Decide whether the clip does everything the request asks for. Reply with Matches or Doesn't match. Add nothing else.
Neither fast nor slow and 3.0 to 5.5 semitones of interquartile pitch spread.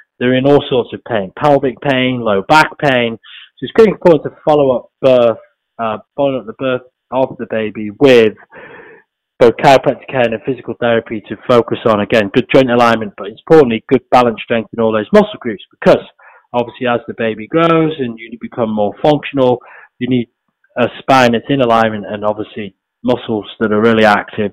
Matches